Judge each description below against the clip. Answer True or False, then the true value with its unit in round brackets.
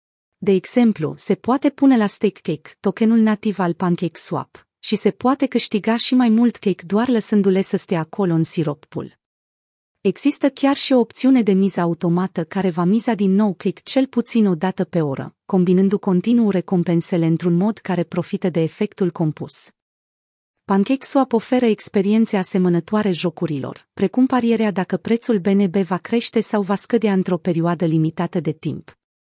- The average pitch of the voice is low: False (195 Hz)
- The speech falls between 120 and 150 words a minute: False (165 wpm)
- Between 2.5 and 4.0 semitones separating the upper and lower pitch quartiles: False (4.4 semitones)